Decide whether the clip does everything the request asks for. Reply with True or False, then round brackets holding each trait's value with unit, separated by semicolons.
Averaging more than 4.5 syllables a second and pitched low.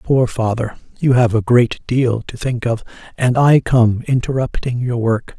False (4.3 syllables/s; 120 Hz)